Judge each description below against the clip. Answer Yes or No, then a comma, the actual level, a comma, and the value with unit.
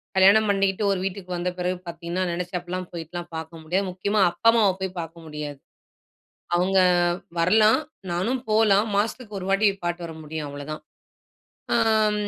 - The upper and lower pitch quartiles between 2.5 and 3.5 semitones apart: Yes, average, 3.1 semitones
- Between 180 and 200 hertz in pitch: Yes, medium, 185 Hz